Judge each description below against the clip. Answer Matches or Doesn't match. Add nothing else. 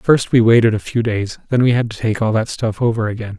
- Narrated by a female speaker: Doesn't match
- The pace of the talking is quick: Matches